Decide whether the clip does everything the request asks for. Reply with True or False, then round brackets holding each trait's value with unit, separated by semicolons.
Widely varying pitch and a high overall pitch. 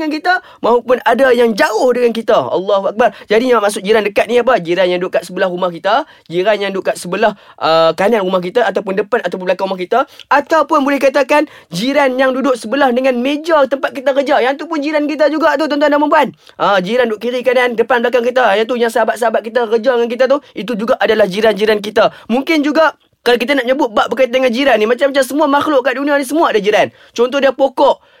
False (4.5 semitones; 250 Hz)